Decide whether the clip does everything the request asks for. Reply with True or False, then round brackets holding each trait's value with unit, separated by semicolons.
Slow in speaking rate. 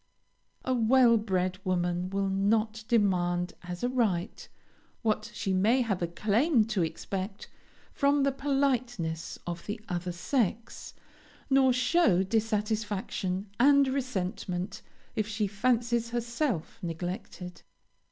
True (115 wpm)